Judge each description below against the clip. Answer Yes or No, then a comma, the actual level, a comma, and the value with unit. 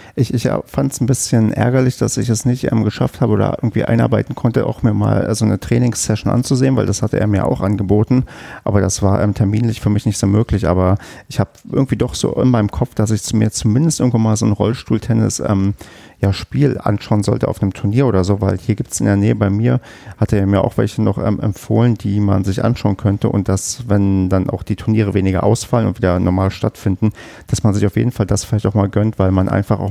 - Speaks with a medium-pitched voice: No, low, 110 Hz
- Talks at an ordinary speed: No, fast, 240 wpm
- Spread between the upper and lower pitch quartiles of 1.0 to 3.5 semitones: Yes, average, 2.8 semitones